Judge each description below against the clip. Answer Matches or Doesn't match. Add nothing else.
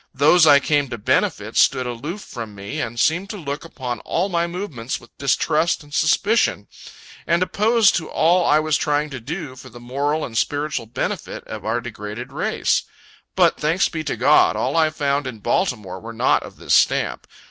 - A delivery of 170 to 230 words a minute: Matches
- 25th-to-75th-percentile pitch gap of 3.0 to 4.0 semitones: Doesn't match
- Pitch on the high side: Doesn't match